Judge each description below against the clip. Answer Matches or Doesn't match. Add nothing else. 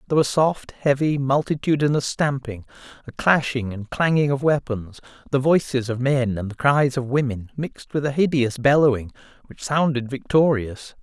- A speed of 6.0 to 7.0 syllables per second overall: Doesn't match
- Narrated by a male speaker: Matches